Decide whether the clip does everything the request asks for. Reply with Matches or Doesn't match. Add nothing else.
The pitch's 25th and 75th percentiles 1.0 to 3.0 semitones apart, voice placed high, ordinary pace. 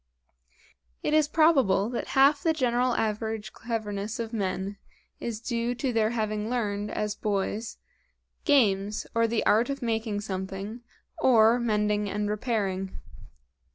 Doesn't match